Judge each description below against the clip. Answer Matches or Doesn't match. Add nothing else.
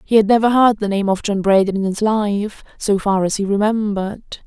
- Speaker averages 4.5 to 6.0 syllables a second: Matches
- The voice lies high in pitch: Matches